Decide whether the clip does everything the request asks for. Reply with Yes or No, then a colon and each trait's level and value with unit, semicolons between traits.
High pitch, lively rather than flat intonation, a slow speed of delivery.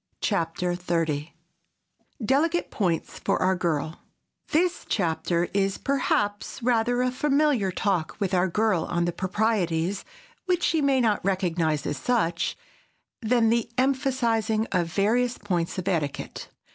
Yes: high, 200 Hz; wide, 6.1 semitones; slow, 120 wpm